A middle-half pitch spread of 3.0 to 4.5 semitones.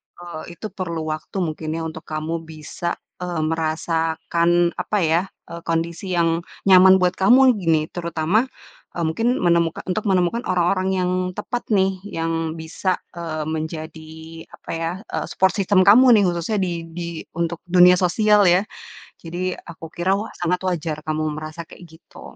No: narrow, 2.4 semitones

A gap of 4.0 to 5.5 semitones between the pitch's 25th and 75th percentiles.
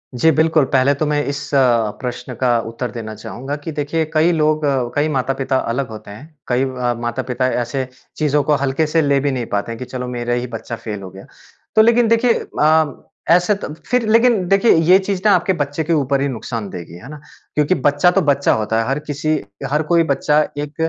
Yes: average, 4.3 semitones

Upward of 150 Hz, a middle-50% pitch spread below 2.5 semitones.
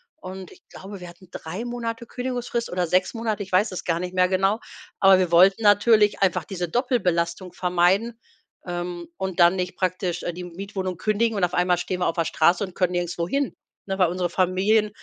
No: medium, 185 Hz; average, 2.8 semitones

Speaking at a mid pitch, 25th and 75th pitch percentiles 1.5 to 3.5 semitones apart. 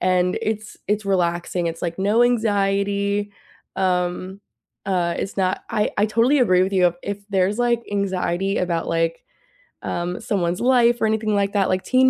No: high, 195 Hz; average, 2.8 semitones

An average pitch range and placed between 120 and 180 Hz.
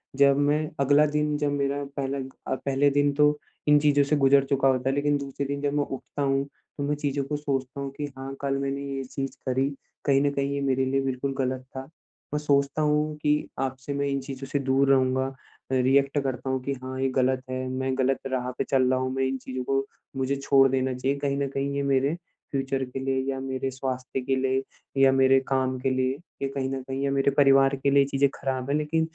No: narrow, 1.0 semitones; low, 135 Hz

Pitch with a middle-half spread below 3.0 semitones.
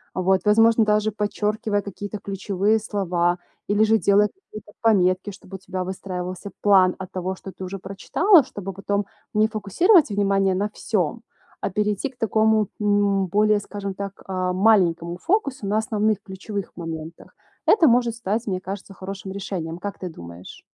Yes: narrow, 2.4 semitones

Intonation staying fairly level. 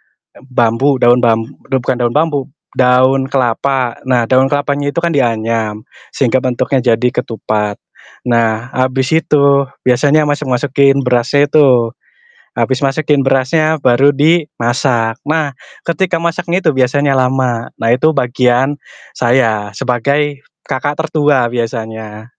No: average, 3.1 semitones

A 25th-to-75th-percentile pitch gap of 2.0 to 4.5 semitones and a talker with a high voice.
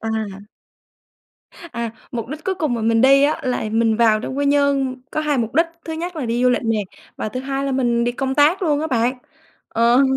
Yes: average, 3.7 semitones; very high, 255 Hz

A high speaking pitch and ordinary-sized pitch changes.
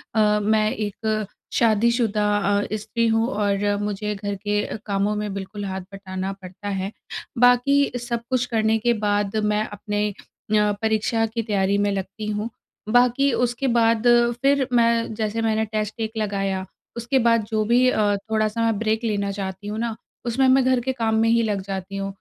No: high, 215 Hz; narrow, 2.3 semitones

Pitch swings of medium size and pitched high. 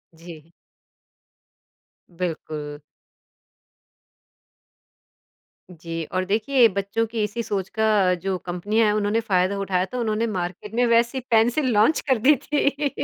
Yes: average, 4.1 semitones; high, 210 Hz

